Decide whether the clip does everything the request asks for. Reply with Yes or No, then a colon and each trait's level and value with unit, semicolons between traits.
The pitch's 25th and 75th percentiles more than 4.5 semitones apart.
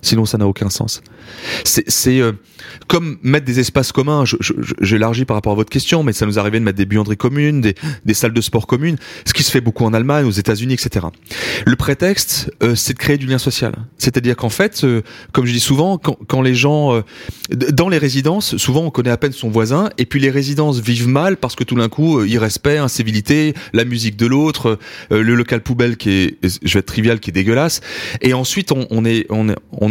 No: average, 4.2 semitones